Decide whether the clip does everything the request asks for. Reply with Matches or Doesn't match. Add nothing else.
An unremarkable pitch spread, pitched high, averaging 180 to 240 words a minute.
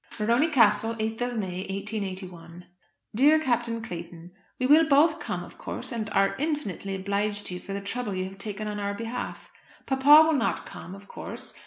Matches